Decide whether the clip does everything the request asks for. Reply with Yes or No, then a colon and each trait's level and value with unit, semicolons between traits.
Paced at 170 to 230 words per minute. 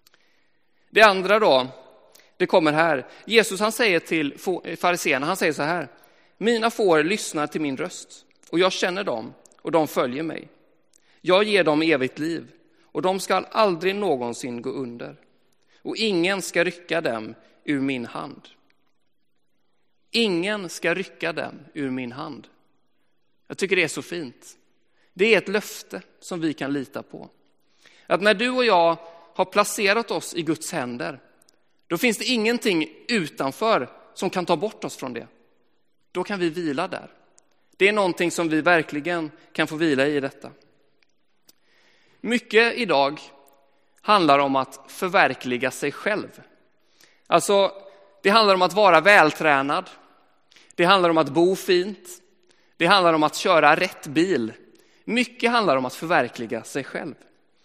No: average, 150 wpm